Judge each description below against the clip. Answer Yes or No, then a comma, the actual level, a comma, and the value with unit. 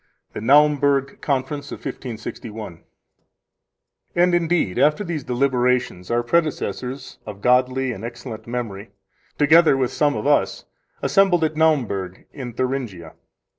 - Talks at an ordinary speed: No, slow, 125 wpm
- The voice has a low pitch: Yes, low, 130 Hz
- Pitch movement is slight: No, average, 4.0 semitones